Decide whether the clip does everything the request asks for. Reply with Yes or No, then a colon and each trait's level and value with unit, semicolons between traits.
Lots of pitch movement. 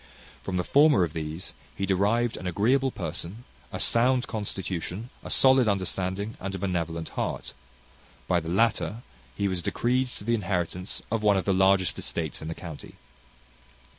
No: average, 4.4 semitones